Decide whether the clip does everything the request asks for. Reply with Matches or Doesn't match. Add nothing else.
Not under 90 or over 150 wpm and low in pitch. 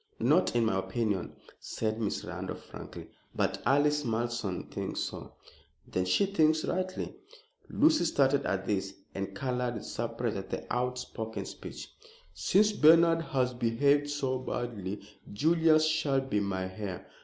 Matches